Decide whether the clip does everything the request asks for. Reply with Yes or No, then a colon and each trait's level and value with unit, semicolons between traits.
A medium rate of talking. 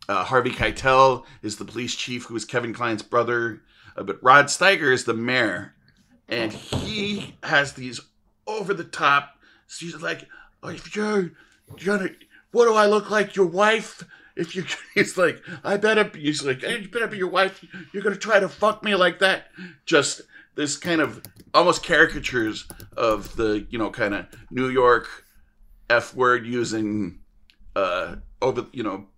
Yes: average, 170 wpm